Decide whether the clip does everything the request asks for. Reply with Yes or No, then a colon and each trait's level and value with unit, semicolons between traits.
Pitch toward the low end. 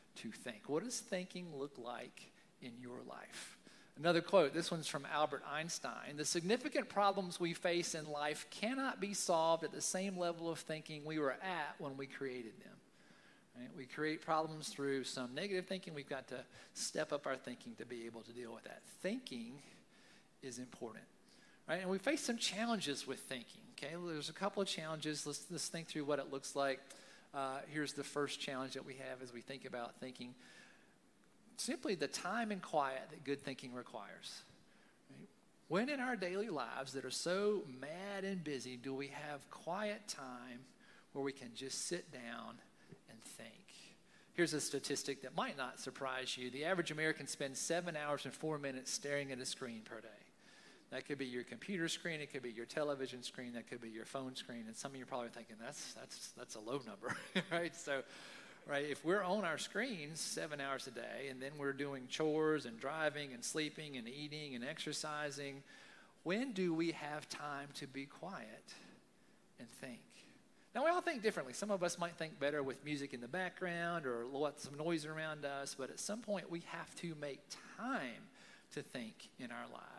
No: medium, 145 Hz